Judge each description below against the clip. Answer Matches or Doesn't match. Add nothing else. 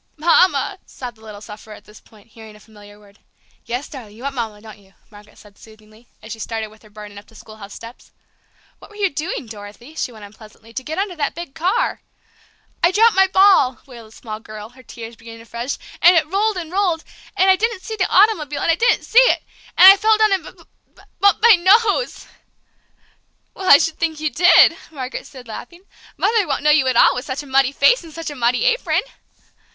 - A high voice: Matches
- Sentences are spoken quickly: Matches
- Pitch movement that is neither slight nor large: Doesn't match